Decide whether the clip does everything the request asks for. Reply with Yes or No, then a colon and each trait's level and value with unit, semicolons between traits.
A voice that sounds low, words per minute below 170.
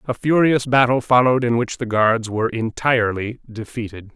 Yes: low, 120 Hz; average, 160 wpm